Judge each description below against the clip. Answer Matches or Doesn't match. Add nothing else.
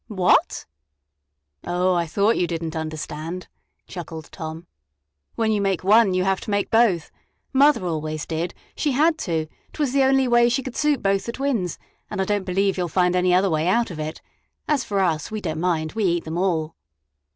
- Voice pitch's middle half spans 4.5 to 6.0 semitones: Matches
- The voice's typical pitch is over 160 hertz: Matches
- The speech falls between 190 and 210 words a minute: Matches